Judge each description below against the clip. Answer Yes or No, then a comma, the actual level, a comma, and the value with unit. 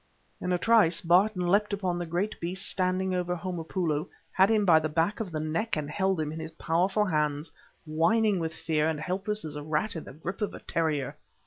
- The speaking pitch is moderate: Yes, medium, 175 Hz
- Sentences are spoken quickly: Yes, fast, 215 wpm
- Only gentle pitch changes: No, average, 3.4 semitones